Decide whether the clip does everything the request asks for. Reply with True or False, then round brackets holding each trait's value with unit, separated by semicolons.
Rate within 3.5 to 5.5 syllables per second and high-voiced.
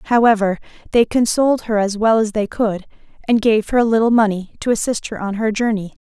False (5.9 syllables/s; 220 Hz)